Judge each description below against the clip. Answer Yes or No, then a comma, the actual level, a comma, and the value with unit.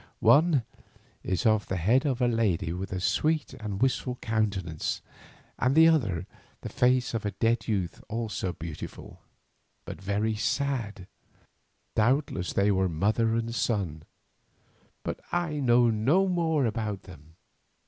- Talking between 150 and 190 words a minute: No, average, 140 wpm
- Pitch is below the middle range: Yes, low, 110 Hz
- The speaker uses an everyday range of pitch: Yes, average, 5.0 semitones